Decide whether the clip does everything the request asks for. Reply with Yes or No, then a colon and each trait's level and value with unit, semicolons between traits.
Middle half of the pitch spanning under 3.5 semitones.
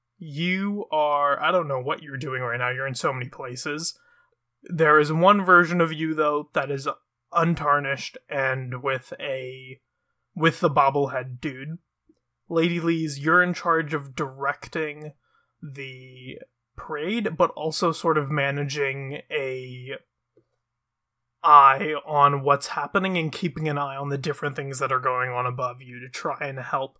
No: average, 3.8 semitones